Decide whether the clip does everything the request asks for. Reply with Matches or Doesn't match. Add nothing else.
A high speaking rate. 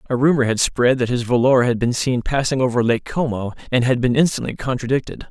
Matches